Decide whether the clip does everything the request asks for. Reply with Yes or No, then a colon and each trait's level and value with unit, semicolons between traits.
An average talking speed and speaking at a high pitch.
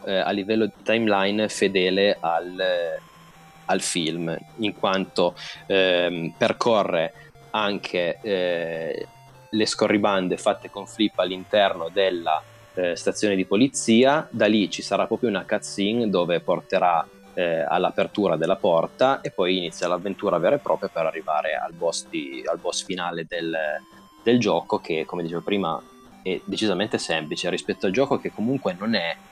No: average, 145 wpm; very low, 95 Hz